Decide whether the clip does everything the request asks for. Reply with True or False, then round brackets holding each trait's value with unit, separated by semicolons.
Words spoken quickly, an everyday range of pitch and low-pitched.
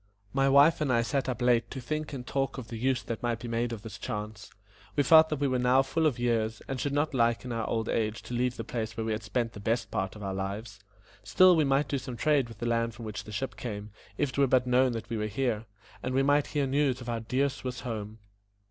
True (275 wpm; 3.3 semitones; 120 Hz)